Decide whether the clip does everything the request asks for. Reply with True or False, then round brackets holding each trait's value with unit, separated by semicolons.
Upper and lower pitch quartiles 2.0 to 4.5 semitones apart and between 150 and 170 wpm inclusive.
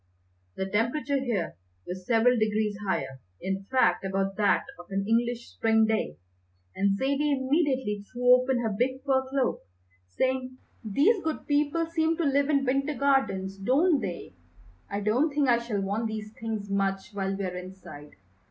False (5.6 semitones; 160 wpm)